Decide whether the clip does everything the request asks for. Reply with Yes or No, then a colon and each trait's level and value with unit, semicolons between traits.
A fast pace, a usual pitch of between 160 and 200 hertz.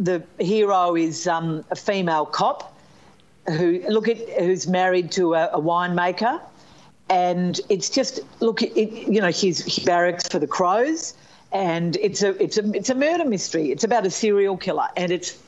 No: average, 170 wpm; medium, 185 Hz